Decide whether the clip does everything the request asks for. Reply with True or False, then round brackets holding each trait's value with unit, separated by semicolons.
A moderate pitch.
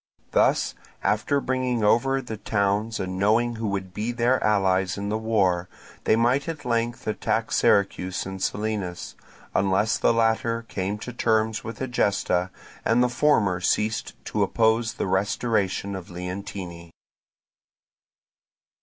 False (110 Hz)